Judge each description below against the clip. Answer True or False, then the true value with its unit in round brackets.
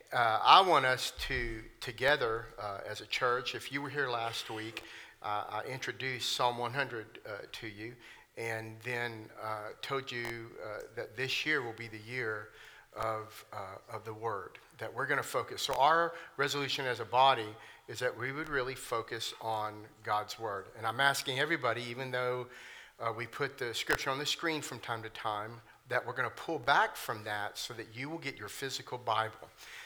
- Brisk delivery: False (195 wpm)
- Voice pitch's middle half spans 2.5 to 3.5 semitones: True (3.0 semitones)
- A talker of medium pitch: False (120 Hz)